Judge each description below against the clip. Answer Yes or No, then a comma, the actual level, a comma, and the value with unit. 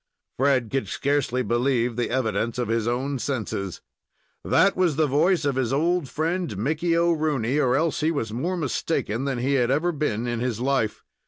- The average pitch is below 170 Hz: Yes, low, 135 Hz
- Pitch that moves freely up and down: No, average, 4.5 semitones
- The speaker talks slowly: No, average, 180 wpm